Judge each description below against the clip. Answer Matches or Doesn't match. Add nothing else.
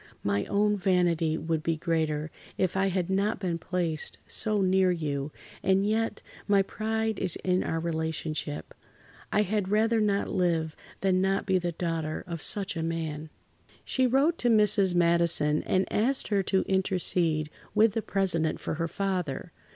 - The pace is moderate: Matches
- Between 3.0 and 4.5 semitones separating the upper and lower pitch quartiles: Matches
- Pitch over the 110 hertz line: Matches